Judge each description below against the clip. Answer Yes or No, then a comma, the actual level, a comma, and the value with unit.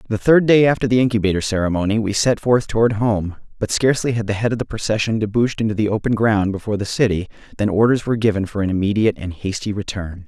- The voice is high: No, low, 110 Hz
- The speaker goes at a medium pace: No, fast, 220 wpm